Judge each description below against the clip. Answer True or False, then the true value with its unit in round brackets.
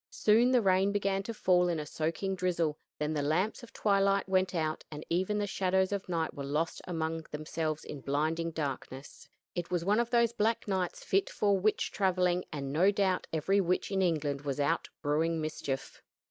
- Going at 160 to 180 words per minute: False (195 wpm)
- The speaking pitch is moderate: True (180 Hz)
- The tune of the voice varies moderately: True (4.0 semitones)